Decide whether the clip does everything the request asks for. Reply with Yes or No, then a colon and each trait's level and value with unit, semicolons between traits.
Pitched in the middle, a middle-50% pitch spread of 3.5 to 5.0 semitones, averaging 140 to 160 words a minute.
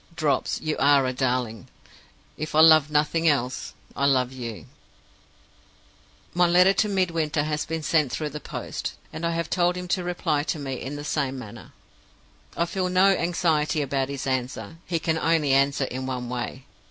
No: medium, 150 Hz; average, 4.0 semitones; average, 175 wpm